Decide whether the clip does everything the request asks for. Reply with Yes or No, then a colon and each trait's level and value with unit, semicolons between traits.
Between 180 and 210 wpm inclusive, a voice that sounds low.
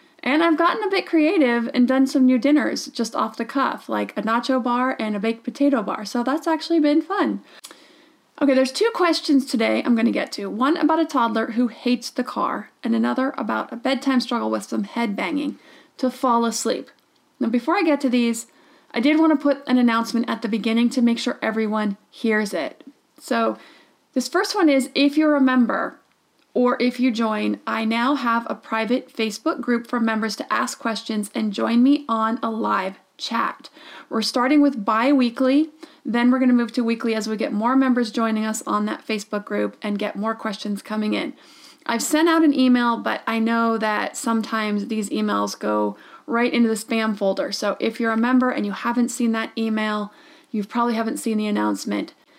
No: average, 200 wpm; high, 245 Hz